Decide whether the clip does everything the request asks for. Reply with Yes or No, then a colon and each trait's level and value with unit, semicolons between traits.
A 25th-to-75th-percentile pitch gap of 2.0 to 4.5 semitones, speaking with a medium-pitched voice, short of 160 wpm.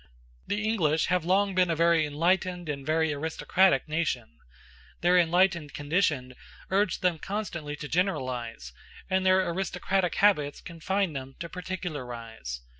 Yes: average, 4.1 semitones; medium, 170 Hz; slow, 135 wpm